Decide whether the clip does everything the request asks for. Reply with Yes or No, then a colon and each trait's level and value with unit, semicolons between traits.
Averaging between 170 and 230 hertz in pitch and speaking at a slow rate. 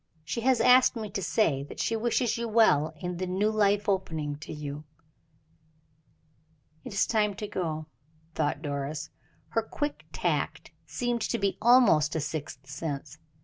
No: medium, 185 Hz; average, 155 wpm